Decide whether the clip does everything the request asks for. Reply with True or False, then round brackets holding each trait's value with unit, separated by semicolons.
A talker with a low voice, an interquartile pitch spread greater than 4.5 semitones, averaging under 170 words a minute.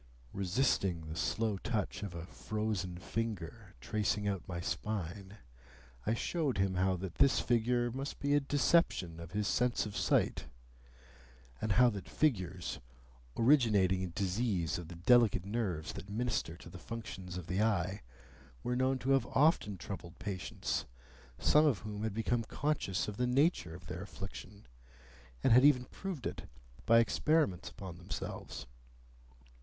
True (105 Hz; 5.1 semitones; 155 wpm)